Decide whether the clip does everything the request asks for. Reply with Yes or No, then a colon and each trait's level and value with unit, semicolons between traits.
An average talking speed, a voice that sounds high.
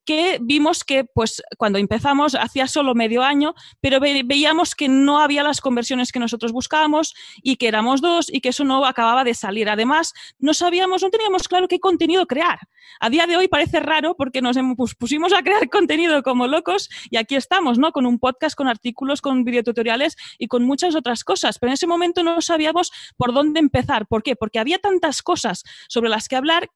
No: fast, 200 wpm; very high, 285 Hz